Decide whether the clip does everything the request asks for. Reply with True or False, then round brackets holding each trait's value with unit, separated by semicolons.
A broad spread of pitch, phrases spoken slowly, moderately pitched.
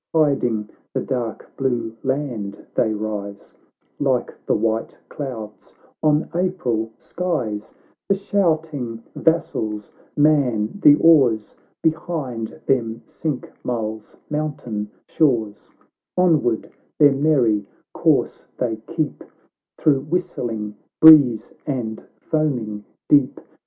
False (5.7 semitones; 95 wpm; 125 Hz)